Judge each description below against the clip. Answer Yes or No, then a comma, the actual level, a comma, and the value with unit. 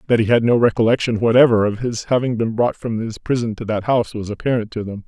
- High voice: No, low, 115 Hz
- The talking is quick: Yes, fast, 250 wpm